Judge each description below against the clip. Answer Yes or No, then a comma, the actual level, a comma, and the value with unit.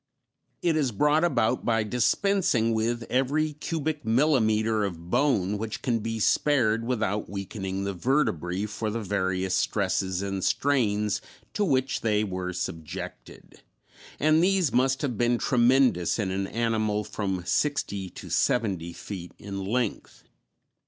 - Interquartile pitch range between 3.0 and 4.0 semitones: No, average, 5.2 semitones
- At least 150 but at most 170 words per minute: No, slow, 135 wpm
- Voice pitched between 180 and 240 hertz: No, low, 110 Hz